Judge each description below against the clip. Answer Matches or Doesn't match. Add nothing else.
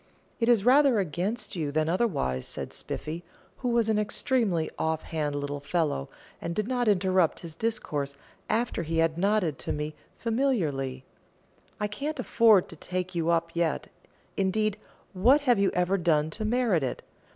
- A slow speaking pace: Doesn't match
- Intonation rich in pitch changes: Matches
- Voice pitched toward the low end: Doesn't match